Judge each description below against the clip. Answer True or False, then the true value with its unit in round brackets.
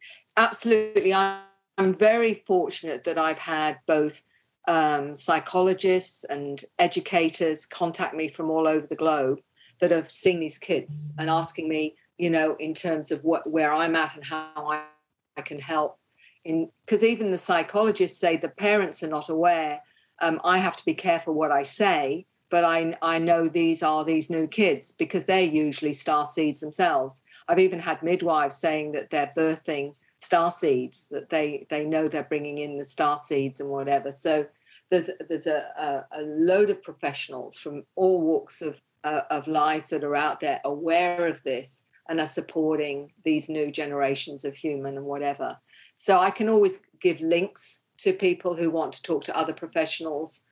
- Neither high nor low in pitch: True (160 Hz)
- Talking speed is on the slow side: False (175 wpm)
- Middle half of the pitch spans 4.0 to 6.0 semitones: False (2.6 semitones)